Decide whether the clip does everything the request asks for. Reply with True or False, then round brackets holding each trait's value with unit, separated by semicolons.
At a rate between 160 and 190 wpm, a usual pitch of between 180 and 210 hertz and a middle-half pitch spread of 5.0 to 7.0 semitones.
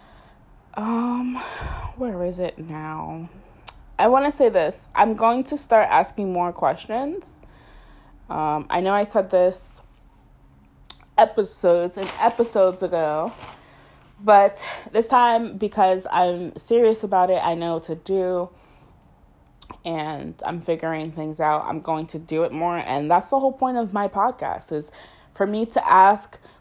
False (145 wpm; 185 Hz; 5.5 semitones)